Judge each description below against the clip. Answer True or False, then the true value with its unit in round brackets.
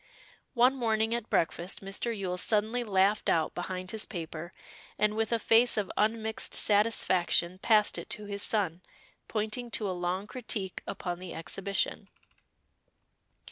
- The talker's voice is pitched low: False (205 Hz)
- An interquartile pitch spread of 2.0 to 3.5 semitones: True (3.2 semitones)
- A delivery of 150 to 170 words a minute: False (140 wpm)